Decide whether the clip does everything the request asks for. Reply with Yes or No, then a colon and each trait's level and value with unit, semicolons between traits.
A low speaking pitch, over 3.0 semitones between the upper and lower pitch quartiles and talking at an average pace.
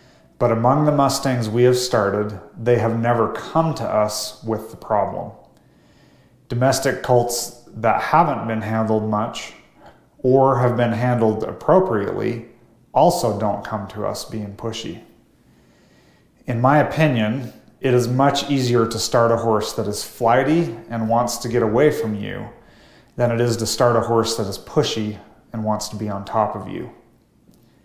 No: low, 115 Hz; narrow, 2.4 semitones; average, 160 wpm